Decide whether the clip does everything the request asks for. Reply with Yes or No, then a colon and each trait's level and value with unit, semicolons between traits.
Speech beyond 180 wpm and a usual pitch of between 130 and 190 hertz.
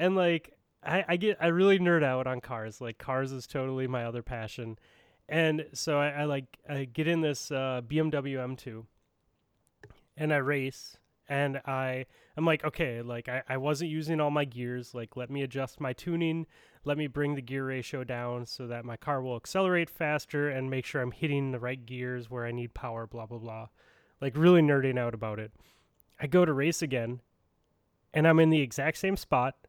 Yes: average, 200 wpm; low, 135 Hz